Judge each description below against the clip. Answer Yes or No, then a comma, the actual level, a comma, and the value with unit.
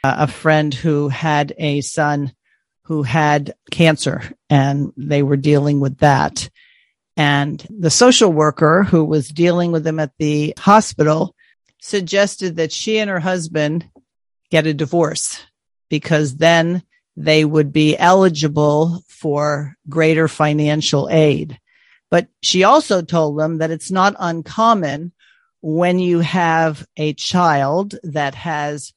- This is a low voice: No, medium, 155 Hz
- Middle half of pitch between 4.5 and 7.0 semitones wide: No, average, 2.8 semitones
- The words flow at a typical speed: No, slow, 130 wpm